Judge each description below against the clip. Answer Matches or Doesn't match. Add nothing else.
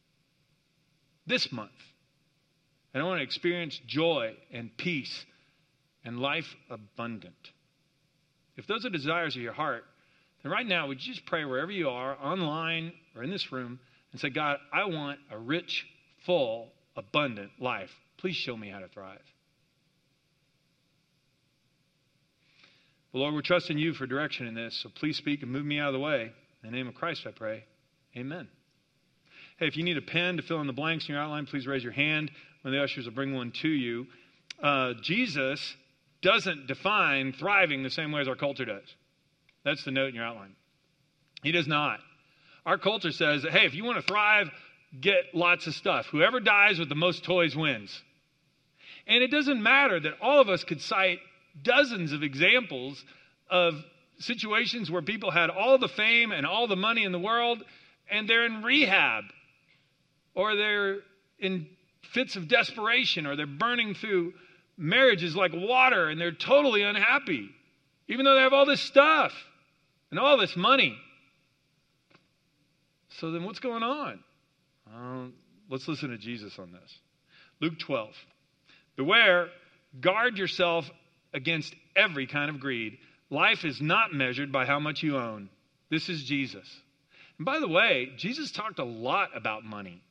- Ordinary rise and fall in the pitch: Matches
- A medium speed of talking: Matches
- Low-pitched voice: Doesn't match